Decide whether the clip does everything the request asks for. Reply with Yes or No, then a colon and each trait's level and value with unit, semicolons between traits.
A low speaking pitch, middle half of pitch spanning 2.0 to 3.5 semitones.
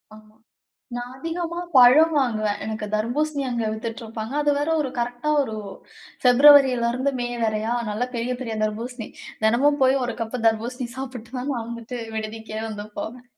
No: high, 245 Hz; average, 3.0 semitones